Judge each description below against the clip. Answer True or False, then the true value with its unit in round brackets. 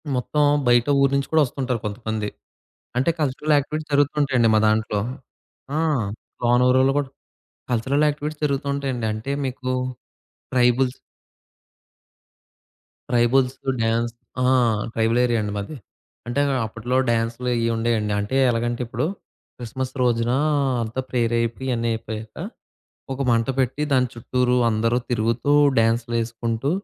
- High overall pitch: False (120 Hz)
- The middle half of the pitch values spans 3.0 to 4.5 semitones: False (2.6 semitones)